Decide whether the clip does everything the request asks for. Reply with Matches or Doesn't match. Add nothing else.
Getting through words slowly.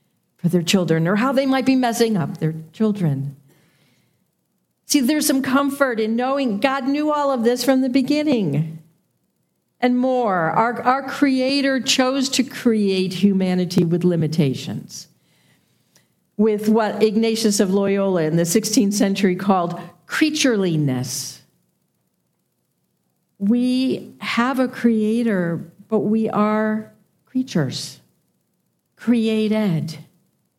Matches